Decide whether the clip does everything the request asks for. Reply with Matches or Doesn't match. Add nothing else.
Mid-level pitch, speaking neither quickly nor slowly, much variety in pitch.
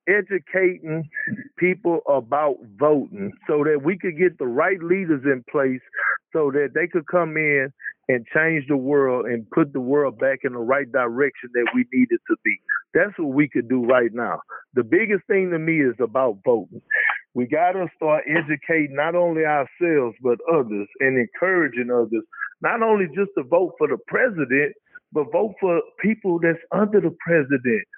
Matches